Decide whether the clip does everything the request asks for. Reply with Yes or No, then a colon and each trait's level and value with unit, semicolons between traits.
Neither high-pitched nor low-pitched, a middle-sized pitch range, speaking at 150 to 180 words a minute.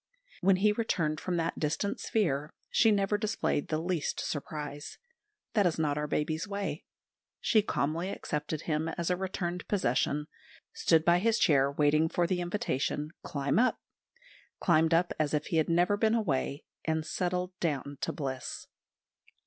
Yes: medium, 165 Hz; average, 3.9 semitones; average, 155 wpm